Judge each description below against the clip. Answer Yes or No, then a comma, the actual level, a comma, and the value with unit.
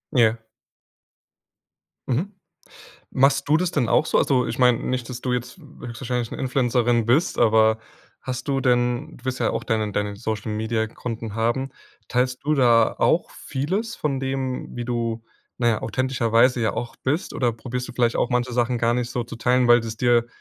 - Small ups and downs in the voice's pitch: Yes, narrow, 2.1 semitones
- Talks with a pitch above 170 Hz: No, low, 125 Hz